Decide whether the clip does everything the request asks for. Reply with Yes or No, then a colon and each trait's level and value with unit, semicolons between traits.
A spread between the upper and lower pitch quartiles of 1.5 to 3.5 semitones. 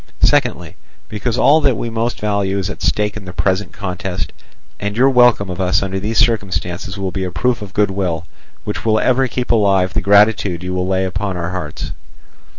Yes: average, 3.0 semitones